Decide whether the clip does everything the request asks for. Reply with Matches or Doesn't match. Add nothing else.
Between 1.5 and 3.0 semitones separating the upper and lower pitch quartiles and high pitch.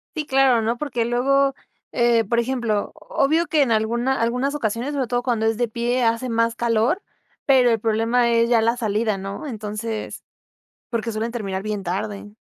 Matches